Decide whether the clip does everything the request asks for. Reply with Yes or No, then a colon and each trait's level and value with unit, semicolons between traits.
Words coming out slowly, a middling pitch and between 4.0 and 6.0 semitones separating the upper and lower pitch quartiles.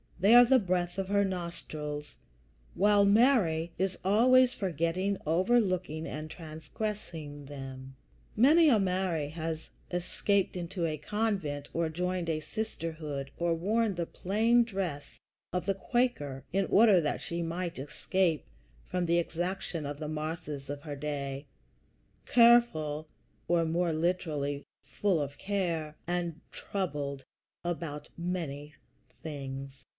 Yes: slow, 125 wpm; medium, 170 Hz; average, 4.4 semitones